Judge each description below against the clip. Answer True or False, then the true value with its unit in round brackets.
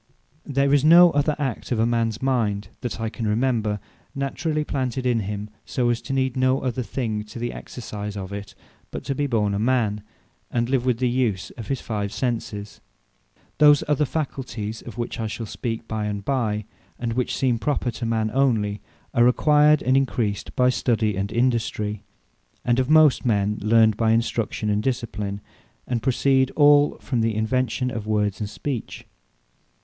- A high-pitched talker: False (120 Hz)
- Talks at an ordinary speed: True (175 wpm)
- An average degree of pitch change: True (3.6 semitones)